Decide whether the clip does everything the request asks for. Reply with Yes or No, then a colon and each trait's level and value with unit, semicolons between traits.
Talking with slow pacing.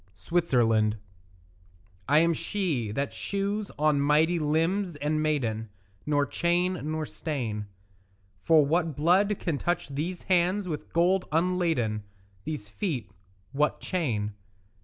Yes: slow, 115 wpm